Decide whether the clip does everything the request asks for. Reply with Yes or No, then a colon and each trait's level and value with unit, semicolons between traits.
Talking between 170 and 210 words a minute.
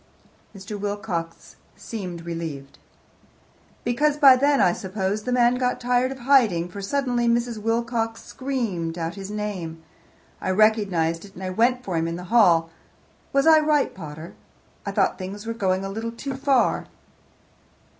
No: average, 155 wpm